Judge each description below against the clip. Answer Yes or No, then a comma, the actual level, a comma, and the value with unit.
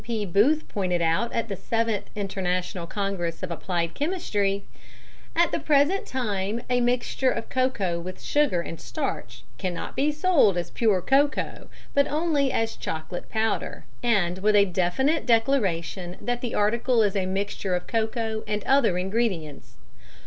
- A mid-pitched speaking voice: No, high, 210 Hz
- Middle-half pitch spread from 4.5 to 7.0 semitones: Yes, wide, 5.4 semitones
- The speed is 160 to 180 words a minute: No, average, 150 wpm